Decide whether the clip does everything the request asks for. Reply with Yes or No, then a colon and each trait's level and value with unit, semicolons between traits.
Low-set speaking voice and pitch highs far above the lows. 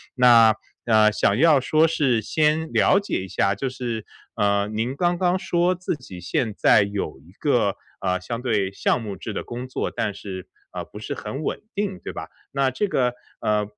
Yes: low, 120 Hz; wide, 6.7 semitones